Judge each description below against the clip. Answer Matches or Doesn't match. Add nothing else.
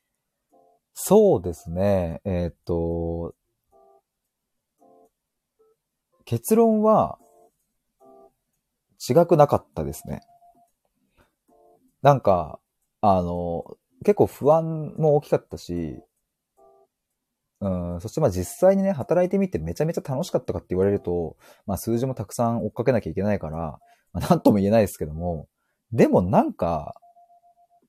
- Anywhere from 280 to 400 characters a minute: Doesn't match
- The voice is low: Matches